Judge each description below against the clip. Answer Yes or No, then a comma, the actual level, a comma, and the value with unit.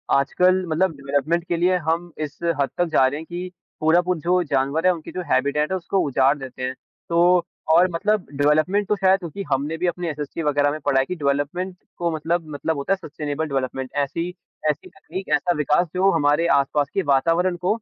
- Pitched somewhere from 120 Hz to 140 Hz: No, medium, 160 Hz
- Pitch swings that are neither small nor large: Yes, average, 3.9 semitones